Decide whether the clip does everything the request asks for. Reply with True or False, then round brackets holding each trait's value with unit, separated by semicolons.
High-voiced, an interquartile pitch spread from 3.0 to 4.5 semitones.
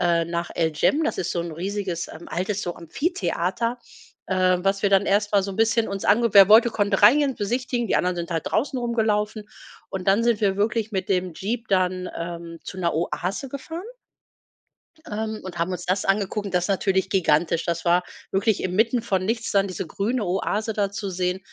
True (195 Hz; 3.5 semitones)